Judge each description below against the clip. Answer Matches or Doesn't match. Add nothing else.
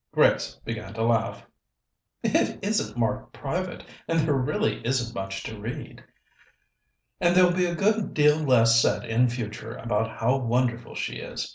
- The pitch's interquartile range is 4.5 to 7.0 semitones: Matches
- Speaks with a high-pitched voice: Doesn't match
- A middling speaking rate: Matches